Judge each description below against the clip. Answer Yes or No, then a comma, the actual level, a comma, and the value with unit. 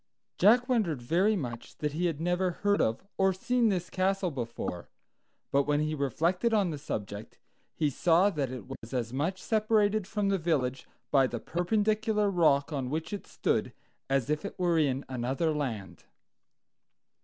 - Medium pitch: Yes, medium, 165 Hz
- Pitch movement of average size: No, wide, 6.5 semitones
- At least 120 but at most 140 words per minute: No, average, 165 wpm